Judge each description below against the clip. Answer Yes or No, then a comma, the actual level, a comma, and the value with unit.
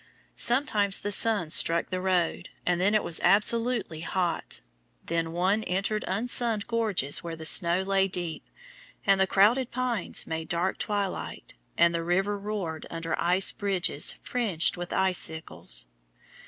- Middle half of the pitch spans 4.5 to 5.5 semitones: No, average, 3.6 semitones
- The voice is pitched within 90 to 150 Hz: No, high, 190 Hz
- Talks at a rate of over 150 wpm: No, average, 140 wpm